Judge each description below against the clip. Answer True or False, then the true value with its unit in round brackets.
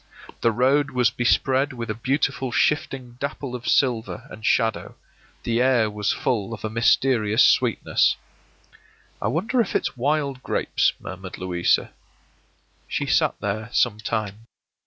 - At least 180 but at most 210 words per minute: False (135 wpm)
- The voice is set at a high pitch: False (120 Hz)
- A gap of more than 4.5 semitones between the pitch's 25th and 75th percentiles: False (3.6 semitones)